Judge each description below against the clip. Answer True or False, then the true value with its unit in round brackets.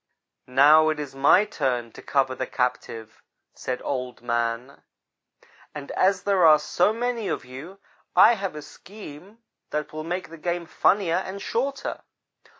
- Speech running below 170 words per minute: True (150 wpm)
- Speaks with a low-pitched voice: False (155 Hz)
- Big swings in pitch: True (6.7 semitones)